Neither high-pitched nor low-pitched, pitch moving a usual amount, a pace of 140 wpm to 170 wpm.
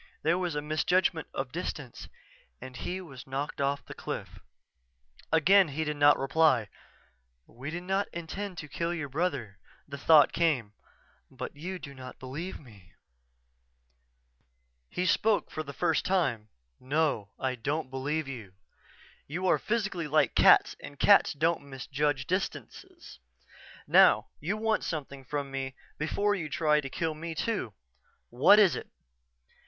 Yes: medium, 150 Hz; average, 4.3 semitones; average, 145 wpm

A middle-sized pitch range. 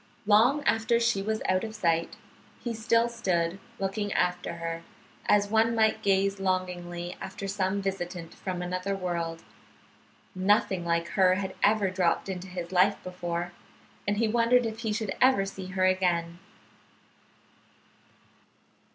Yes: average, 3.3 semitones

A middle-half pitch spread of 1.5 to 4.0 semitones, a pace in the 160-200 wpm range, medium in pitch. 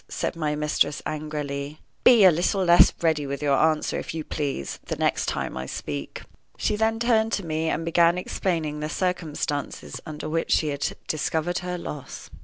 Yes: average, 3.0 semitones; average, 180 wpm; medium, 155 Hz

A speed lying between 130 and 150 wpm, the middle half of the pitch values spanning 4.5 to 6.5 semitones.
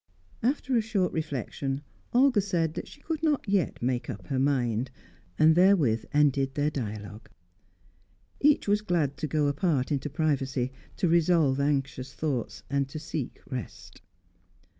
Yes: average, 145 wpm; average, 5.1 semitones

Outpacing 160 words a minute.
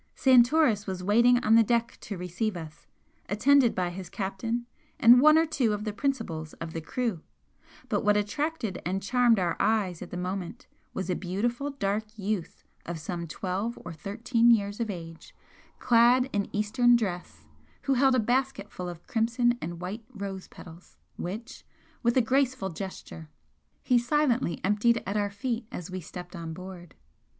Yes: average, 170 wpm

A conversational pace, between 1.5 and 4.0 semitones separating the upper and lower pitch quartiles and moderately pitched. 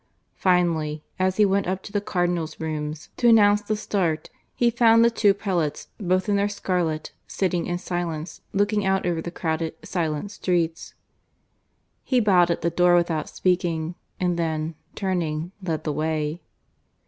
Yes: average, 160 wpm; average, 3.6 semitones; medium, 175 Hz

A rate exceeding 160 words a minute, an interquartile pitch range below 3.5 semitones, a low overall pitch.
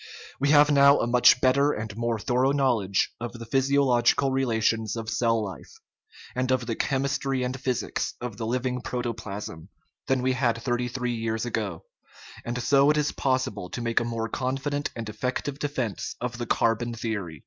Yes: average, 180 wpm; average, 2.8 semitones; low, 120 Hz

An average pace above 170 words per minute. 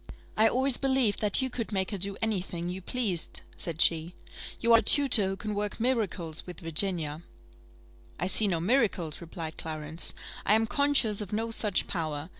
Yes: average, 180 wpm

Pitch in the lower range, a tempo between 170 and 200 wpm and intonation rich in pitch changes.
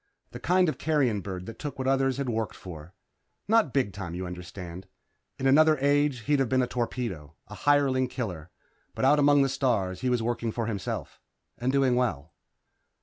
Yes: low, 125 Hz; average, 190 wpm; wide, 6.3 semitones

